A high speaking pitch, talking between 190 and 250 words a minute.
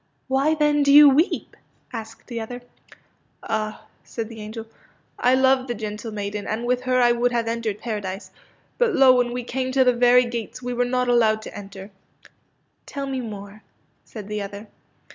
Yes: high, 240 Hz; average, 200 wpm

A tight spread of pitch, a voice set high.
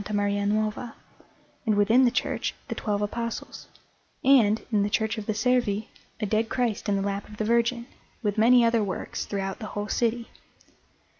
Yes: narrow, 2.3 semitones; high, 215 Hz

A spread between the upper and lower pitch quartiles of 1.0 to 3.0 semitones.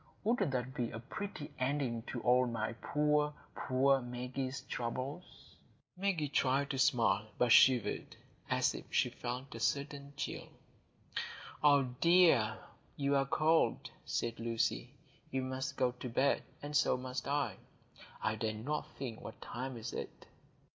Yes: average, 2.7 semitones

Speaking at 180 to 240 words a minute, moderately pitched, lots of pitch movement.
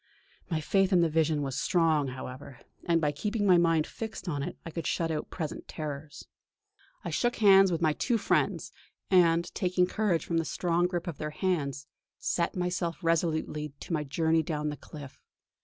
No: average, 185 wpm; medium, 165 Hz; average, 2.9 semitones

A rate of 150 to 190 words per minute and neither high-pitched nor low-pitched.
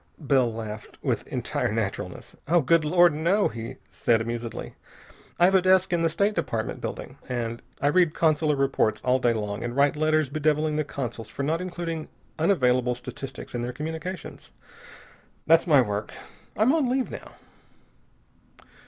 Yes: average, 155 wpm; medium, 150 Hz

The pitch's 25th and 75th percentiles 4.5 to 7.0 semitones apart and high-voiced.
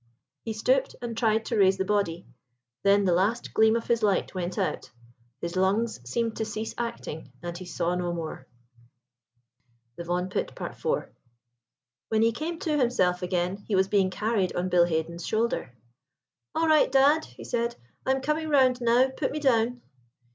Yes: average, 5.1 semitones; high, 215 Hz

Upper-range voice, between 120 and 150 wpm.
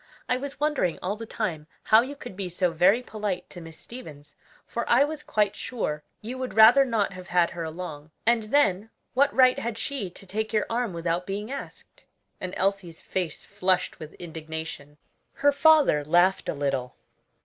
No: high, 195 Hz; average, 180 wpm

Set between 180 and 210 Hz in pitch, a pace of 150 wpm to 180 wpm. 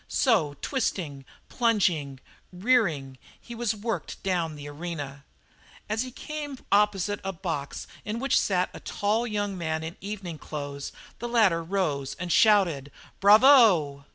No: high, 190 Hz; slow, 135 wpm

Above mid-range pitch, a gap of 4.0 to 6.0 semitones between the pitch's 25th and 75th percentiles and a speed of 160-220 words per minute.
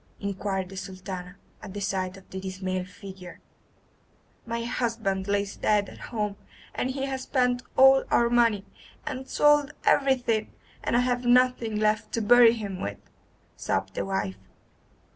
No: high, 210 Hz; average, 4.3 semitones; average, 150 wpm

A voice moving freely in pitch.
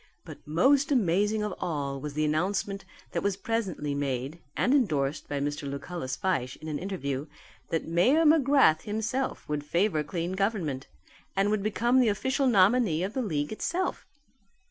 Yes: wide, 6.7 semitones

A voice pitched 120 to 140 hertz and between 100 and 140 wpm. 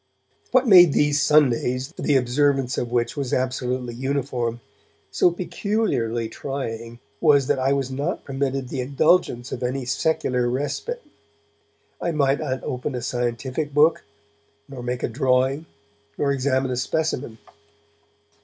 Yes: low, 135 Hz; slow, 135 wpm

